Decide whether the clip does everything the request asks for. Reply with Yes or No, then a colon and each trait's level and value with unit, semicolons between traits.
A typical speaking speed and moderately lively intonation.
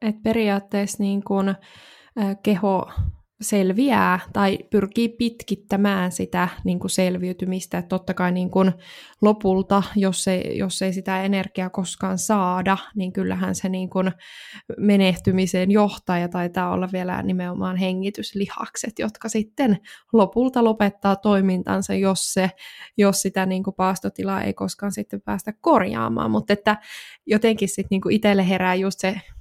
No: average, 135 wpm; narrow, 1.8 semitones